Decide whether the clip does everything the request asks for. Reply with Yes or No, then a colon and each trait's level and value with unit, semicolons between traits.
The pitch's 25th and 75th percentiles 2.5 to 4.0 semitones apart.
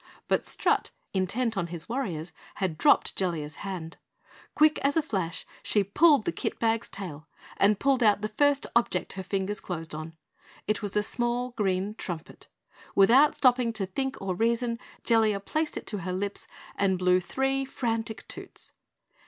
No: average, 4.8 semitones